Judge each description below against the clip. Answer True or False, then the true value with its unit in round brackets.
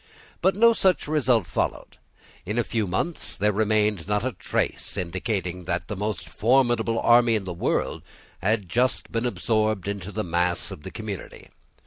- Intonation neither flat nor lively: True (4.1 semitones)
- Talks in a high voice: False (110 Hz)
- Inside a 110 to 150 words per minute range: False (165 wpm)